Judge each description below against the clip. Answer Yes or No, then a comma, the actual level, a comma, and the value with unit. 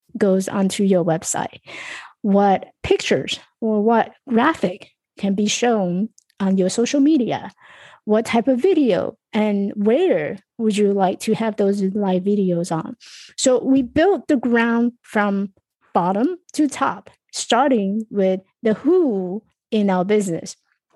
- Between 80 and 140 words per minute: Yes, slow, 135 wpm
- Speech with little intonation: No, average, 3.8 semitones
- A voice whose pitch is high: Yes, high, 215 Hz